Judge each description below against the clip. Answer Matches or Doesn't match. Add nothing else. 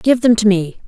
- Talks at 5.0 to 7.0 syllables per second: Matches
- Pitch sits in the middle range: Doesn't match